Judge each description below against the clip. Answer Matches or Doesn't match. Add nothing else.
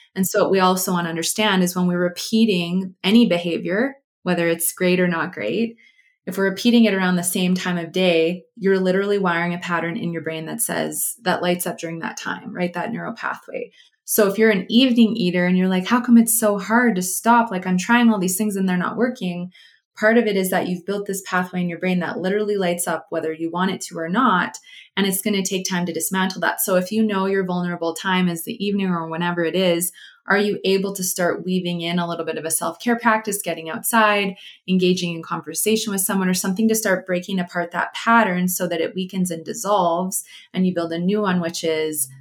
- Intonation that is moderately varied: Matches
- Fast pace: Matches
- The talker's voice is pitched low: Doesn't match